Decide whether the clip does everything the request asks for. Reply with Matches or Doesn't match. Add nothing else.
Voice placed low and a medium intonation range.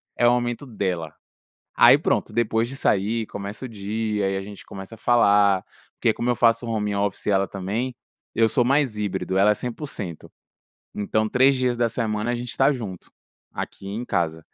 Matches